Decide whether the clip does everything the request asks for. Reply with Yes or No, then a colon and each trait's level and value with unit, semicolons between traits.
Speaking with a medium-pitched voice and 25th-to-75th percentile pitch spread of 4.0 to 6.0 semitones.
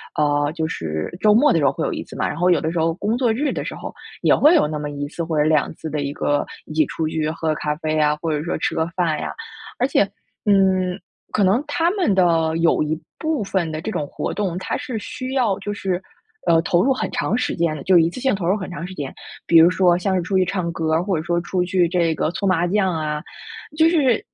Yes: medium, 175 Hz; average, 4.3 semitones